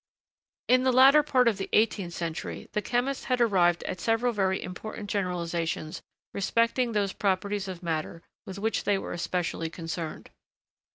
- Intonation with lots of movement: No, average, 4.9 semitones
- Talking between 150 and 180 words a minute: Yes, average, 160 wpm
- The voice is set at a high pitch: Yes, high, 200 Hz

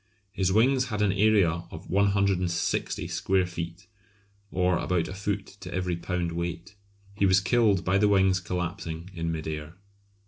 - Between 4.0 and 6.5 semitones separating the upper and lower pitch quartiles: No, narrow, 2.5 semitones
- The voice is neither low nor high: No, very low, 95 Hz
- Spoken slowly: No, average, 160 wpm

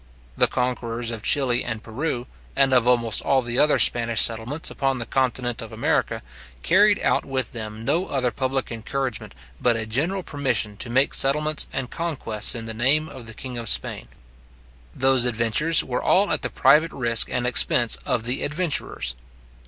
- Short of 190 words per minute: Yes, average, 175 wpm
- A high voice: No, low, 125 Hz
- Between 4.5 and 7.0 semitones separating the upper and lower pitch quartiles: No, average, 3.0 semitones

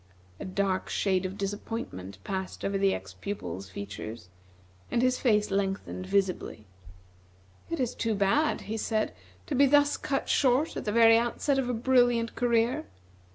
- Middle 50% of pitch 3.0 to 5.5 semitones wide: Yes, average, 4.5 semitones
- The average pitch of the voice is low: No, high, 210 Hz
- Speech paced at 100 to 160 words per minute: Yes, average, 155 wpm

